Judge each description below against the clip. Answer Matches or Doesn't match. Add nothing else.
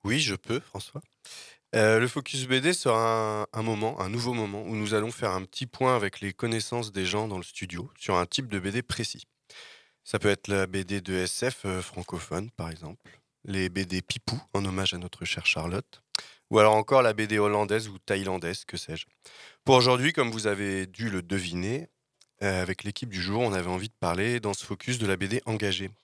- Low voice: Matches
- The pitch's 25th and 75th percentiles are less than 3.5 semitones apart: Doesn't match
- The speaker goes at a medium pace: Matches